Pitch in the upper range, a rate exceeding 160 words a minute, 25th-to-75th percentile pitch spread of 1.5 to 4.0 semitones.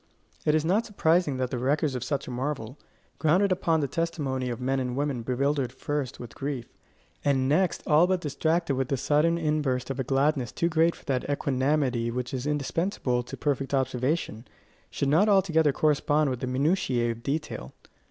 No: medium, 140 Hz; average, 180 wpm; average, 3.5 semitones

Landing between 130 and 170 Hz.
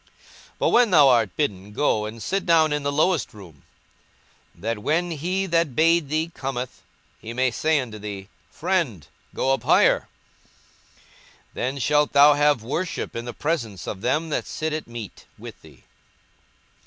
Yes: medium, 140 Hz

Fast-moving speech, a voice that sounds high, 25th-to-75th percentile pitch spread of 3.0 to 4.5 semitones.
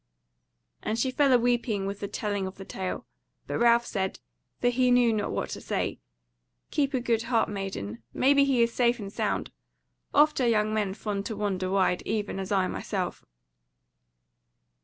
No: average, 180 wpm; high, 220 Hz; average, 3.8 semitones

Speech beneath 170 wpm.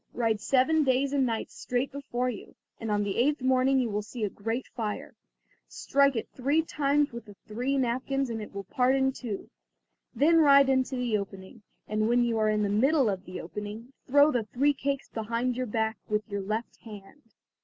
No: average, 200 wpm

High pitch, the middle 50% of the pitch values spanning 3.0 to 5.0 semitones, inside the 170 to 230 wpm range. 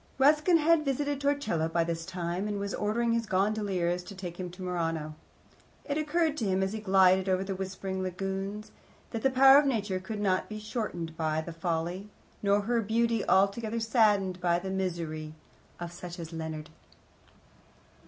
Yes: high, 195 Hz; average, 4.4 semitones; average, 175 wpm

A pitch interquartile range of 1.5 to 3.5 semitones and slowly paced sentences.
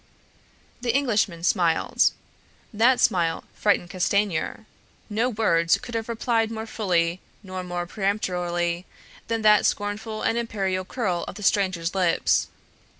No: average, 4.0 semitones; slow, 125 wpm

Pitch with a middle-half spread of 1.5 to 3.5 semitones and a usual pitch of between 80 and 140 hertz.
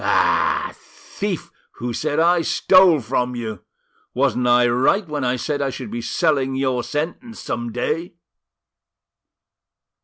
No: average, 5.0 semitones; low, 135 Hz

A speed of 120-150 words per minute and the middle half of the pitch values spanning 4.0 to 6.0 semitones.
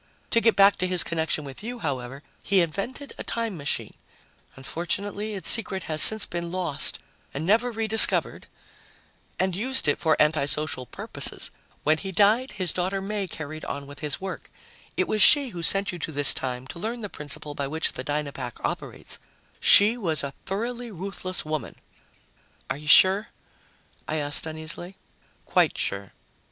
No: average, 165 wpm; average, 5.2 semitones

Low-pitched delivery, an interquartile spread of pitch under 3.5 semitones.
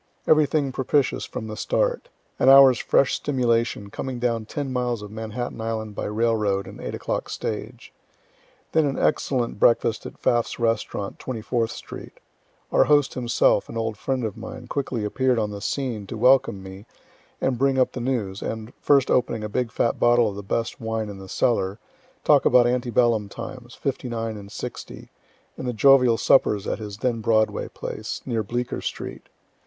Yes: low, 115 Hz; average, 3.0 semitones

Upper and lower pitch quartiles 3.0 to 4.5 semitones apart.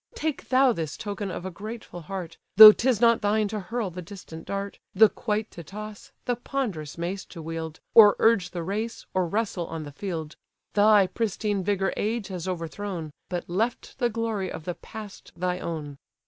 Yes: average, 4.0 semitones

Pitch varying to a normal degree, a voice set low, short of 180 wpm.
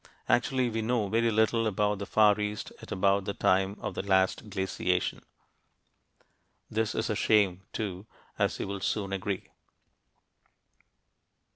No: narrow, 2.3 semitones; low, 105 Hz; average, 140 wpm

